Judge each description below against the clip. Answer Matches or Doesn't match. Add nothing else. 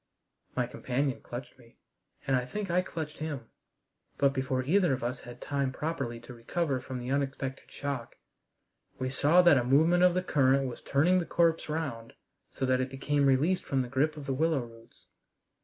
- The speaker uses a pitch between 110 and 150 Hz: Matches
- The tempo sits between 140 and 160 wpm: Doesn't match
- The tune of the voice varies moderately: Matches